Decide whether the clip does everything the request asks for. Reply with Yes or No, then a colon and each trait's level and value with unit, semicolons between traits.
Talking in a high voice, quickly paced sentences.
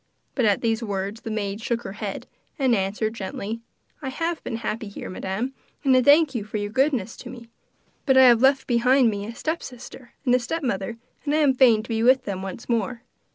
Yes: high, 235 Hz; fast, 215 wpm